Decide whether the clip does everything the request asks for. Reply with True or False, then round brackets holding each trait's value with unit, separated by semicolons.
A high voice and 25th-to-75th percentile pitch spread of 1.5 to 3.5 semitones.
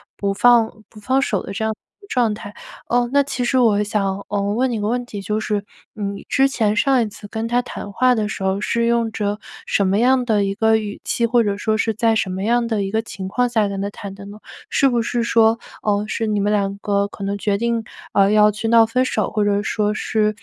True (215 Hz; 2.5 semitones)